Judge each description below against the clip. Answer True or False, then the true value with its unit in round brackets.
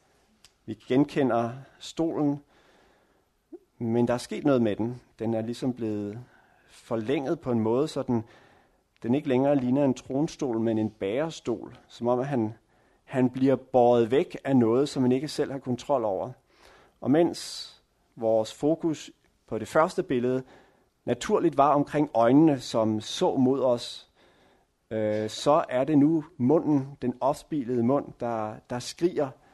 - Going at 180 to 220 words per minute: False (150 wpm)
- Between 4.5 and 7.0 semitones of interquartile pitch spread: False (3.8 semitones)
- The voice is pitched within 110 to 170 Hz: True (125 Hz)